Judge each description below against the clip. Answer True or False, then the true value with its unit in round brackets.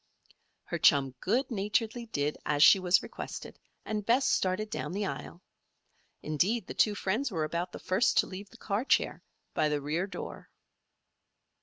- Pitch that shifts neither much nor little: False (5.7 semitones)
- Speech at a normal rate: True (165 wpm)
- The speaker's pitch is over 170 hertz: True (190 Hz)